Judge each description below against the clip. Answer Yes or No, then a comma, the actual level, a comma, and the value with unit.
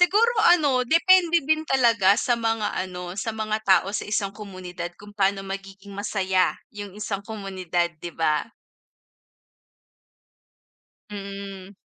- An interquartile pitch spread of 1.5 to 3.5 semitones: Yes, average, 3.2 semitones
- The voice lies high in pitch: Yes, high, 200 Hz